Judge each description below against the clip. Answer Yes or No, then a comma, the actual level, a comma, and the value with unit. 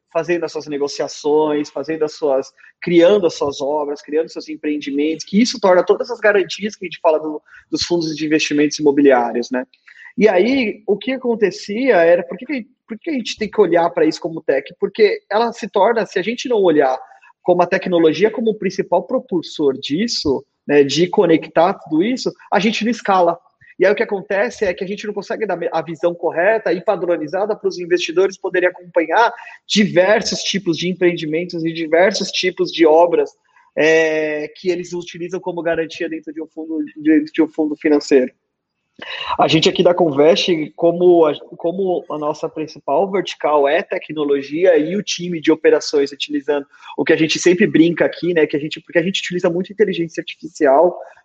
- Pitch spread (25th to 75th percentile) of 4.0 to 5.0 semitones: Yes, average, 4.5 semitones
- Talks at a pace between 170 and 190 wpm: Yes, fast, 185 wpm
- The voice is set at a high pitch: No, medium, 175 Hz